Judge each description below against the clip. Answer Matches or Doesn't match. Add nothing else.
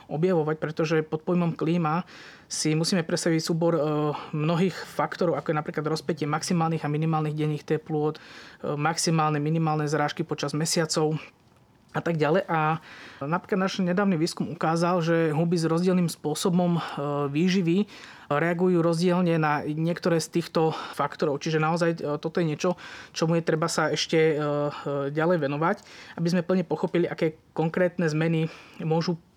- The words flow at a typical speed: Matches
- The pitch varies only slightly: Matches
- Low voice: Doesn't match